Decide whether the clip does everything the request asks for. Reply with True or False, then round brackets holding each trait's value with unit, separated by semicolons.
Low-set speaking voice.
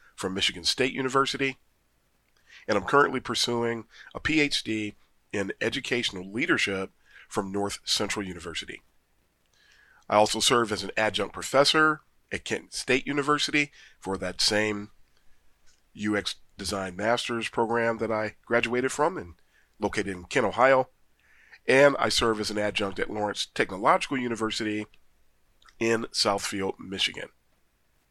True (110 Hz)